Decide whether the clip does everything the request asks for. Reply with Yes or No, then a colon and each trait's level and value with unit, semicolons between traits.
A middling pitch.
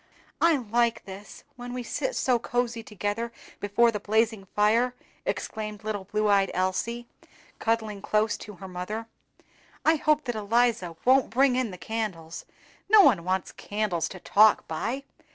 No: high, 220 Hz